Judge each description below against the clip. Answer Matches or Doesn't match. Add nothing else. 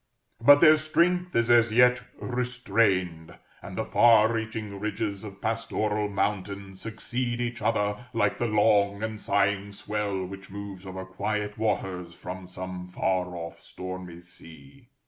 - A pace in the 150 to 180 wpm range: Doesn't match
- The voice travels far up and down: Doesn't match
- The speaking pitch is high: Doesn't match